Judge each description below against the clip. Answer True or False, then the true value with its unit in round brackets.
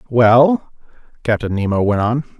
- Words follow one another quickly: False (125 wpm)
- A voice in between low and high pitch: False (115 Hz)